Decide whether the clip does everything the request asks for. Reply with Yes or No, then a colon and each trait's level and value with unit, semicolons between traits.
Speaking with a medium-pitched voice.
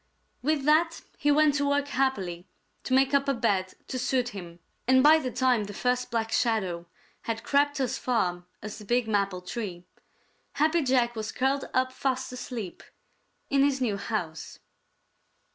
No: very high, 250 Hz